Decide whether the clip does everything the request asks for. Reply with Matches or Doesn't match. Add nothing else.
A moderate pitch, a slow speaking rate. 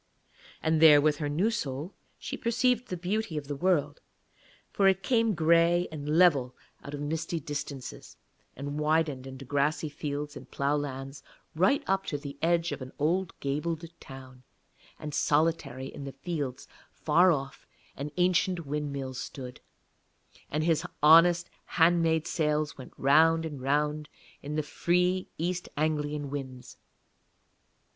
Doesn't match